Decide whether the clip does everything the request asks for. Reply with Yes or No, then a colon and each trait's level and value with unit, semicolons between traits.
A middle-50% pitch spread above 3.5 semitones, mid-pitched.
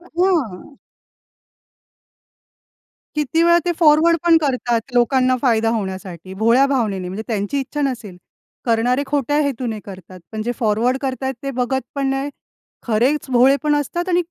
No: average, 4.6 semitones; very high, 255 Hz